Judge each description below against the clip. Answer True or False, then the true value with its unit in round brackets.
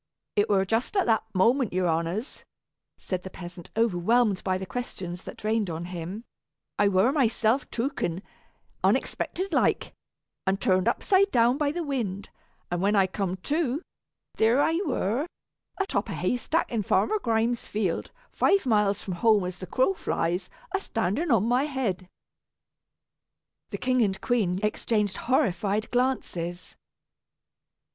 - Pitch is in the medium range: False (215 Hz)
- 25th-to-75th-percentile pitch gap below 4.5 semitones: False (5.4 semitones)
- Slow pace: False (145 wpm)